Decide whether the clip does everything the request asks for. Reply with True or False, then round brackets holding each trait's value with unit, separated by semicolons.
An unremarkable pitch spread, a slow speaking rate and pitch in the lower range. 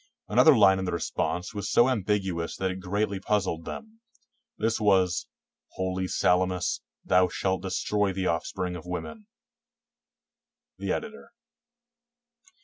False (2.3 semitones; 125 wpm; 95 Hz)